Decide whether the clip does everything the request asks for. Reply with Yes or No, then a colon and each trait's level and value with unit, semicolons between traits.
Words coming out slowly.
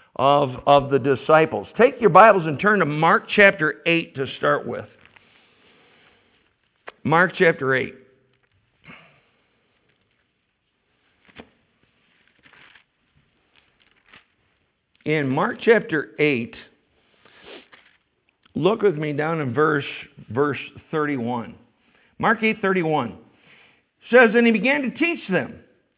Yes: slow, 95 wpm